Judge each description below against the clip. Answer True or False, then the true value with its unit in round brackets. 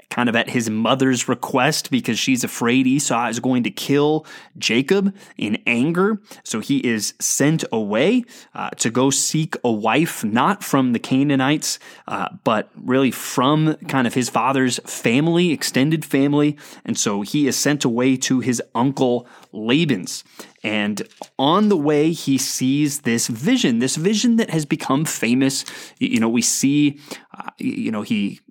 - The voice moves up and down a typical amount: True (4.8 semitones)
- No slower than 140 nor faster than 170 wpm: True (160 wpm)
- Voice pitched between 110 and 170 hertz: True (140 Hz)